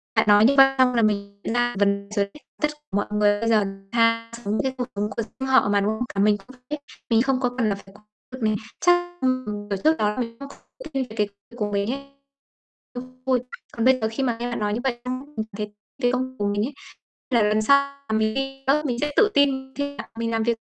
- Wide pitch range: No, average, 4.0 semitones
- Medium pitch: No, high, 235 Hz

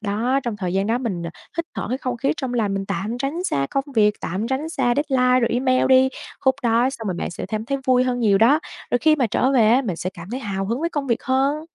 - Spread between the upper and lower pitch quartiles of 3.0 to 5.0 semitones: Yes, average, 4.0 semitones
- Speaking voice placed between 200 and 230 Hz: No, high, 245 Hz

